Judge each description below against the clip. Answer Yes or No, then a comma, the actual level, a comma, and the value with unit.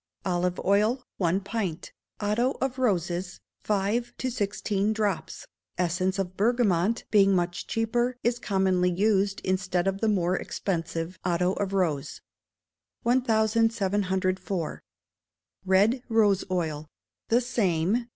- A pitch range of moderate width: Yes, average, 3.6 semitones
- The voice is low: No, high, 195 Hz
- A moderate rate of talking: No, slow, 110 wpm